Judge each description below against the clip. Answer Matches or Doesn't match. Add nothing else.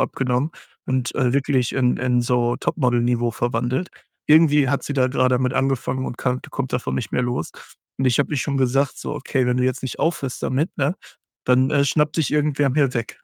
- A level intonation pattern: Matches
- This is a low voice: Matches